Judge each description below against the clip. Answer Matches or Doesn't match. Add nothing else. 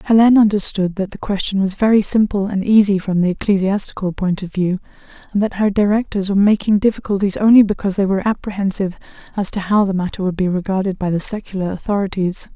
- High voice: Matches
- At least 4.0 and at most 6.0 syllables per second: Doesn't match